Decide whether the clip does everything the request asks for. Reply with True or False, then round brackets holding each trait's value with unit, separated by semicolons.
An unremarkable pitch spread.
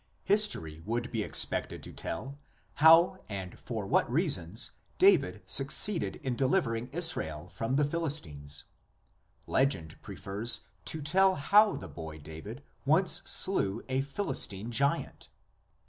False (8.7 semitones)